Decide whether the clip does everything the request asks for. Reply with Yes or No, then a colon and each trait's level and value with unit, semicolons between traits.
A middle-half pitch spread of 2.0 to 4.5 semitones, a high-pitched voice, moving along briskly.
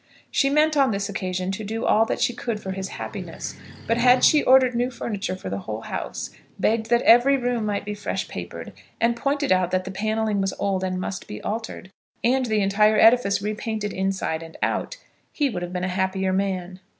Yes: average, 4.0 semitones; high, 210 Hz; fast, 210 wpm